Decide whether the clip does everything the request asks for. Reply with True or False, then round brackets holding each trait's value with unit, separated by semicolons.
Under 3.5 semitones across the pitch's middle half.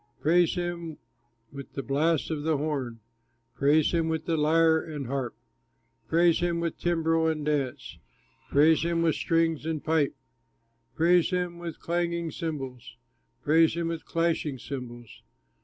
True (2.5 semitones)